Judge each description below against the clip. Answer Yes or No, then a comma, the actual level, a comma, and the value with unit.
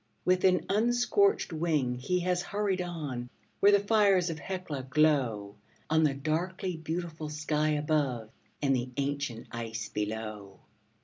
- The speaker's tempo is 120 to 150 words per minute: Yes, slow, 135 wpm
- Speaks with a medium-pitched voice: Yes, medium, 155 Hz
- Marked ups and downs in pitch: Yes, wide, 6.2 semitones